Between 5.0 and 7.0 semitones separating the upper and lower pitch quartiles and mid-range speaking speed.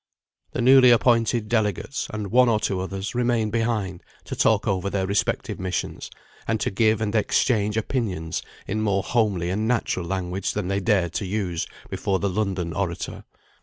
No: average, 3.1 semitones; average, 165 wpm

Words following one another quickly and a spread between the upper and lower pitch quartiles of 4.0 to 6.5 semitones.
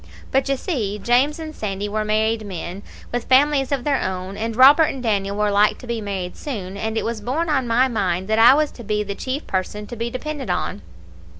Yes: fast, 225 wpm; average, 4.6 semitones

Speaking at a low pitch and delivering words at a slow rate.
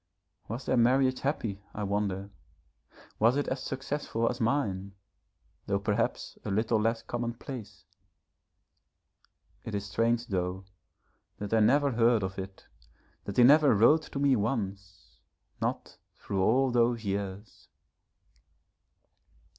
Yes: low, 115 Hz; slow, 125 wpm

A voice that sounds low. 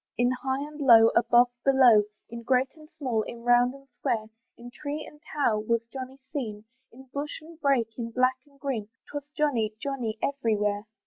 No: very high, 250 Hz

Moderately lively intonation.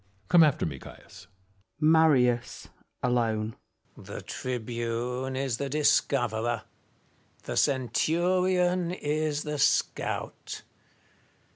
Yes: average, 4.7 semitones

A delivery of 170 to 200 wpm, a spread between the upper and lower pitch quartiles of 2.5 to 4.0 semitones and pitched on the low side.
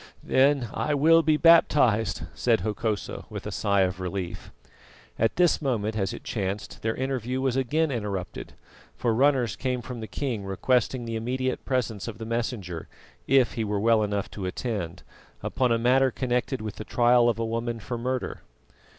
Yes: average, 175 wpm; average, 3.5 semitones; low, 115 Hz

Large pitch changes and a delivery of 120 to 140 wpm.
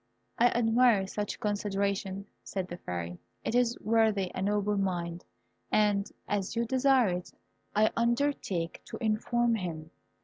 No: average, 3.6 semitones; slow, 135 wpm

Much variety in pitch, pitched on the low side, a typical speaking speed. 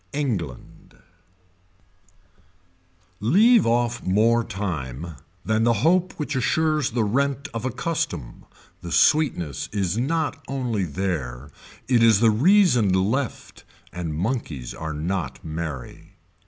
No: wide, 7.7 semitones; low, 110 Hz; slow, 115 wpm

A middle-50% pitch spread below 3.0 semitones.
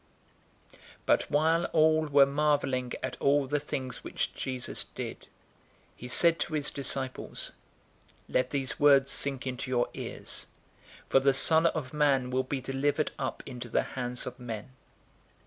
Yes: narrow, 2.4 semitones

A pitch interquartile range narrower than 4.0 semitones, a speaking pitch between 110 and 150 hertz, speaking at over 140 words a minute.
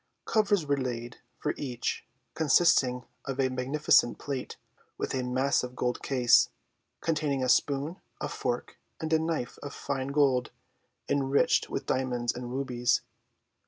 No: average, 2.7 semitones; low, 135 Hz; slow, 135 wpm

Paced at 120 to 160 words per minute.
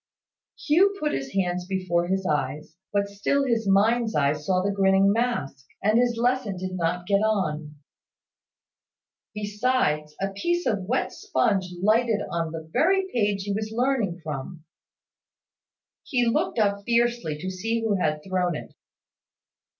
Yes: average, 145 wpm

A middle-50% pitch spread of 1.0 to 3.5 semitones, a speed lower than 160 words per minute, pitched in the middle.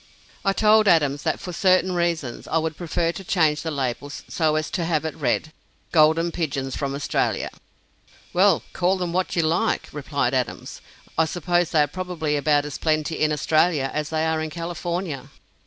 No: average, 2.9 semitones; average, 180 wpm; medium, 160 Hz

